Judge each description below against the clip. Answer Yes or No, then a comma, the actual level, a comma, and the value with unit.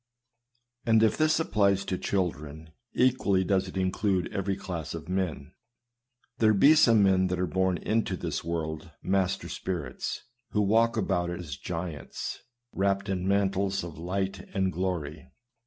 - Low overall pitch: Yes, very low, 95 Hz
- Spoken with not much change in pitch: Yes, narrow, 2.2 semitones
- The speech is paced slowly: No, average, 150 wpm